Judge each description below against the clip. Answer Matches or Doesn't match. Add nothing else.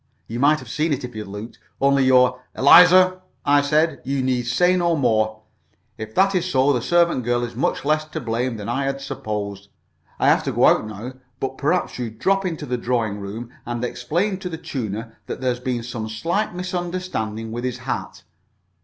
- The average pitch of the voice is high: Doesn't match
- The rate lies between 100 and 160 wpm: Doesn't match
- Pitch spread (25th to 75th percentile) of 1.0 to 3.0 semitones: Doesn't match